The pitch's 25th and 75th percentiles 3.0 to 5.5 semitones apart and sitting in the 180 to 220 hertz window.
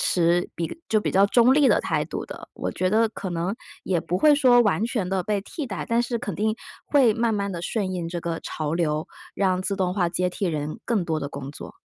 Yes: average, 4.6 semitones; high, 190 Hz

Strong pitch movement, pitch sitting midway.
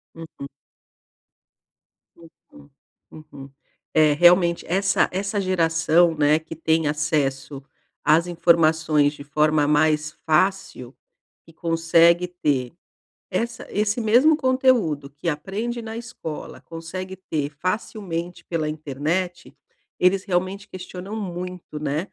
No: average, 3.6 semitones; medium, 165 Hz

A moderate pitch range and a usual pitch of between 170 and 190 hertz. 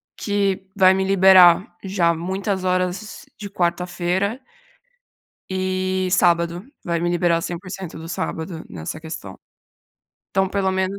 No: narrow, 1.8 semitones; medium, 185 Hz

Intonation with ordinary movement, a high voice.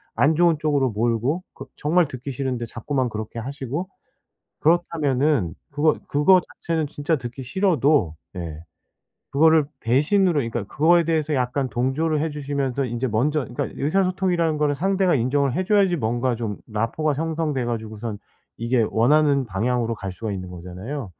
No: average, 5.0 semitones; medium, 140 Hz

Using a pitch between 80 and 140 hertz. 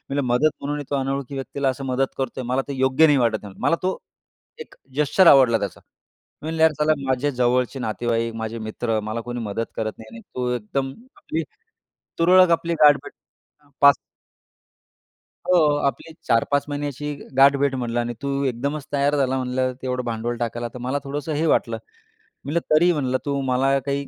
Yes: low, 135 Hz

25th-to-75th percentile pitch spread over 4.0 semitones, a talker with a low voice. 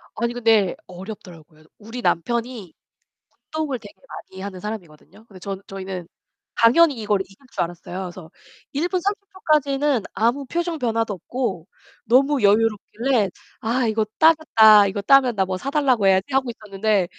No: average, 5.3 semitones; high, 220 Hz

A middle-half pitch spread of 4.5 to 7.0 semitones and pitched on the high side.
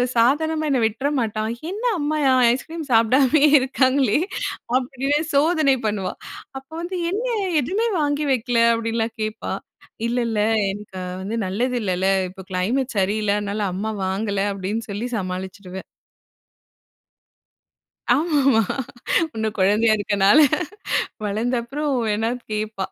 Yes: average, 5.0 semitones; high, 230 Hz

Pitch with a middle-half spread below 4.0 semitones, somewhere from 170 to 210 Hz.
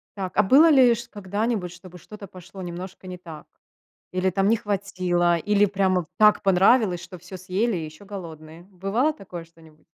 Yes: average, 2.9 semitones; medium, 185 Hz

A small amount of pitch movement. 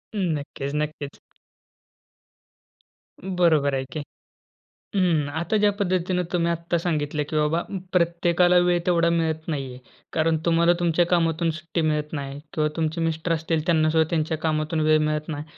Yes: narrow, 2.0 semitones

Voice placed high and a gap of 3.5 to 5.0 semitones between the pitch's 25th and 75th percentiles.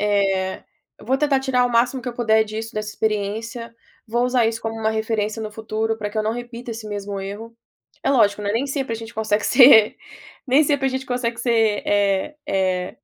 No: high, 225 Hz; narrow, 2.6 semitones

